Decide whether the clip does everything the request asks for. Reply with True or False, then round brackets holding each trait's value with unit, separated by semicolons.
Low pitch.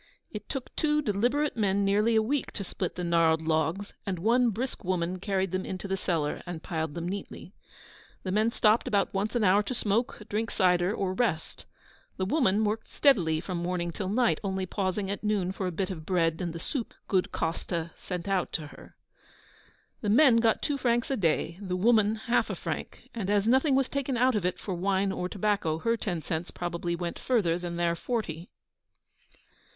False (195 Hz)